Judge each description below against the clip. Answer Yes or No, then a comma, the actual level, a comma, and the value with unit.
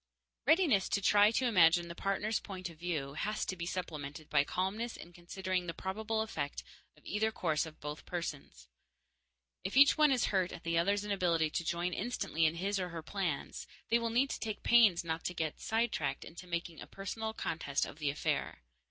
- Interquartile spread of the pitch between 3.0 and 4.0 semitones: No, average, 4.5 semitones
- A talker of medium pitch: Yes, medium, 180 Hz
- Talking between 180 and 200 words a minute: Yes, average, 195 wpm